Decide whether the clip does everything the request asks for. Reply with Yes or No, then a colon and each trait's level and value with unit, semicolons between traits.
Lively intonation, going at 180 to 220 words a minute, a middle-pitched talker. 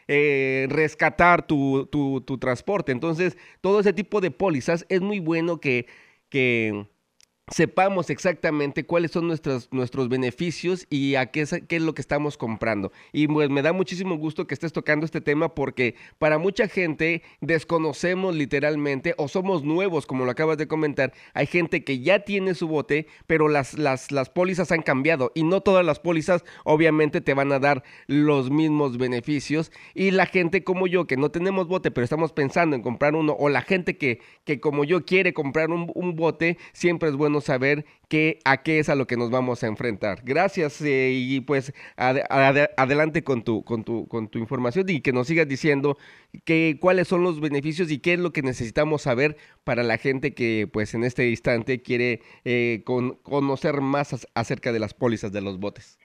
No: average, 4.2 semitones; average, 190 wpm; medium, 150 Hz